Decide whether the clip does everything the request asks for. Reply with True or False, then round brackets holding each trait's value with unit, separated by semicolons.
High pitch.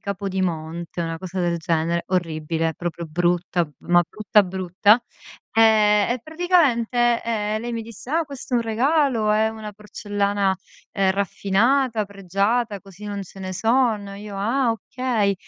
True (205 Hz)